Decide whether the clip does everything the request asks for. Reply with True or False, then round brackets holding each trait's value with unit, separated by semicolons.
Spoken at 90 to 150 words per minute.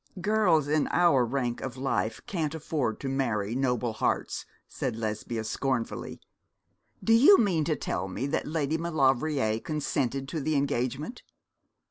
True (140 wpm)